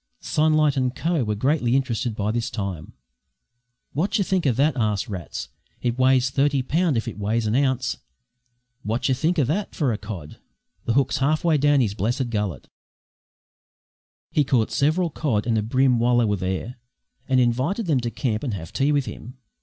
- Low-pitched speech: Yes, low, 125 Hz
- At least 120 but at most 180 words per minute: No, average, 190 wpm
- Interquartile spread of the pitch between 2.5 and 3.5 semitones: No, average, 4.6 semitones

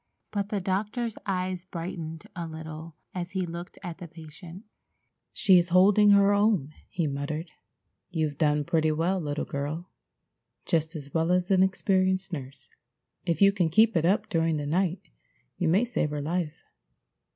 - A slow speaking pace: No, average, 160 wpm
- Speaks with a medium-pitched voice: Yes, medium, 175 Hz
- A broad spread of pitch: No, average, 3.2 semitones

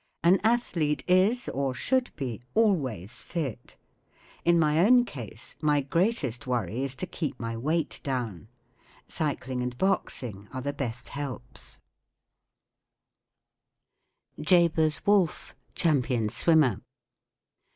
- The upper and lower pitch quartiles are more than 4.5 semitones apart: Yes, wide, 5.6 semitones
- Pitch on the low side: No, medium, 145 Hz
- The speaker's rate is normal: No, slow, 110 wpm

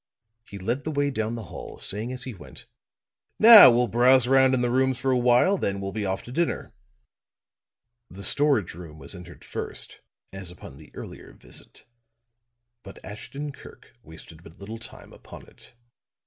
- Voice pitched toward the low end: Yes, low, 115 Hz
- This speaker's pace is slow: No, average, 175 wpm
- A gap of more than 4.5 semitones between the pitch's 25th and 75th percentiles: Yes, wide, 5.4 semitones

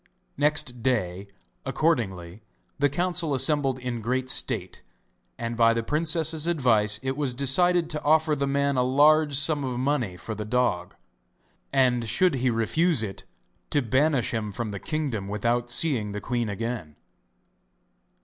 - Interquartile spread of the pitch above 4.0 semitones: Yes, average, 4.7 semitones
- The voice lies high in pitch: No, low, 130 Hz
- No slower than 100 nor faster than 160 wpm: Yes, average, 150 wpm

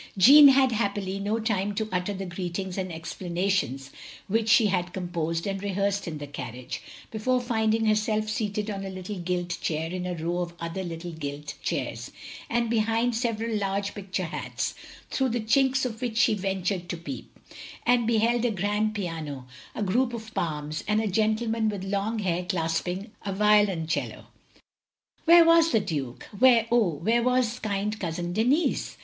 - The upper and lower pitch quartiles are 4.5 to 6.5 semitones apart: No, average, 4.1 semitones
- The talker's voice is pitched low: No, high, 200 Hz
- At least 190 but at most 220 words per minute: No, average, 170 wpm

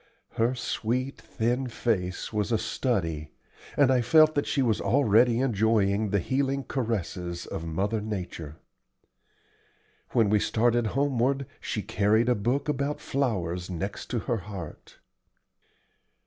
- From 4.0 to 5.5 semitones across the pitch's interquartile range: Yes, average, 4.6 semitones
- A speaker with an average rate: No, slow, 130 wpm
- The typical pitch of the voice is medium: No, low, 115 Hz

